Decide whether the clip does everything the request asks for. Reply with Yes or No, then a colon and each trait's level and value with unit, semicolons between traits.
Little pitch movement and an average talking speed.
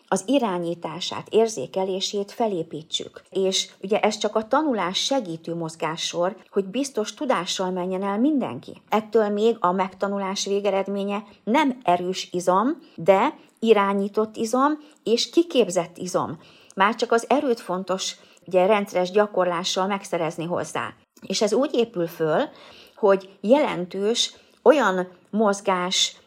No: average, 4.1 semitones; average, 115 wpm